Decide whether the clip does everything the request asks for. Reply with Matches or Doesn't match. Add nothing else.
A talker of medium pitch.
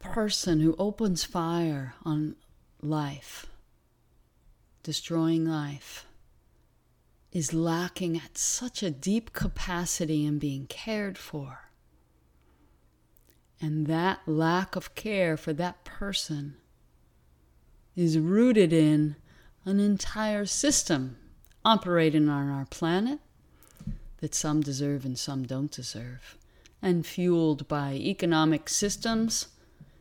Matches